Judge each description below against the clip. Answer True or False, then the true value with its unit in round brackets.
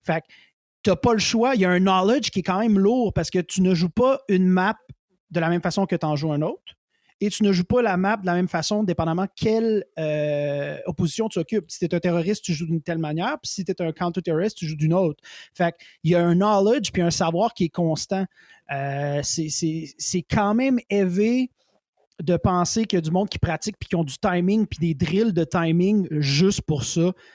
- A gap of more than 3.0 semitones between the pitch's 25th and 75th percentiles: True (3.8 semitones)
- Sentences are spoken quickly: True (250 wpm)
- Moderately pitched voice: True (180 Hz)